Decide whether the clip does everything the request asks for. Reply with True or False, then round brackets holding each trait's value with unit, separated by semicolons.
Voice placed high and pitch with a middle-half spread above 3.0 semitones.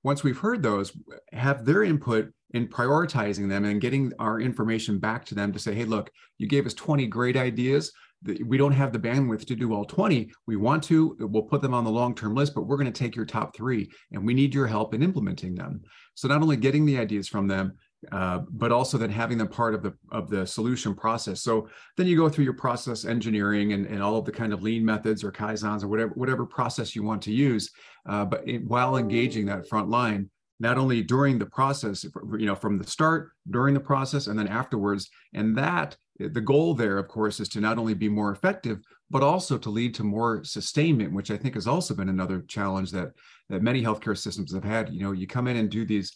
False (115 Hz; 4.1 semitones)